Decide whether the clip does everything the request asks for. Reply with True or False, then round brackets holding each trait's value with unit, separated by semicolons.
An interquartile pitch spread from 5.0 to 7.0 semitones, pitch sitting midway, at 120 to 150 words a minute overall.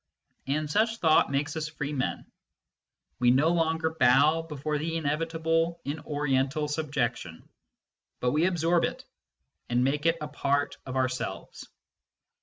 False (2.9 semitones; 150 Hz; 135 wpm)